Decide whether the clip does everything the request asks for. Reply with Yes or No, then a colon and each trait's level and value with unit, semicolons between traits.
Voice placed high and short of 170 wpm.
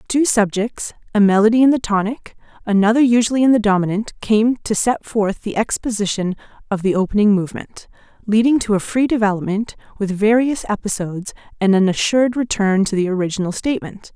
Yes: high, 210 Hz; average, 160 wpm